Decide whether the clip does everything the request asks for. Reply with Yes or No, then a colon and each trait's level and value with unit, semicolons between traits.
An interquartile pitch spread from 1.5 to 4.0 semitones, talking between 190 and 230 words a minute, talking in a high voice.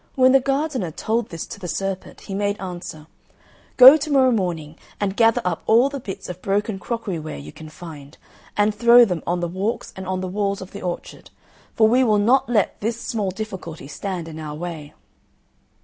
No: average, 4.8 semitones; average, 200 wpm; high, 195 Hz